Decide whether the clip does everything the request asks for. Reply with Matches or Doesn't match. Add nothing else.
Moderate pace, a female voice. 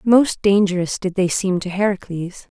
Matches